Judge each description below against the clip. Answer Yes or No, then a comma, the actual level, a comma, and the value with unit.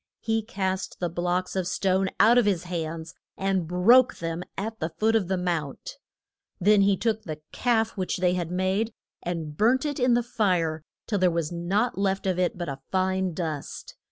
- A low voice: No, medium, 185 Hz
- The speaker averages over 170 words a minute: Yes, average, 190 wpm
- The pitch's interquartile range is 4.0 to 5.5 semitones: No, average, 3.6 semitones